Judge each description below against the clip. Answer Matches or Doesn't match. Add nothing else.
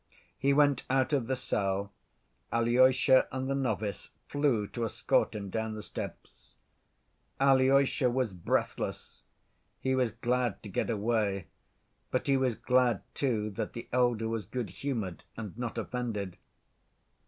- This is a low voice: Matches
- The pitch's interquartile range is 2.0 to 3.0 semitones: Doesn't match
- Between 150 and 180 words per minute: Doesn't match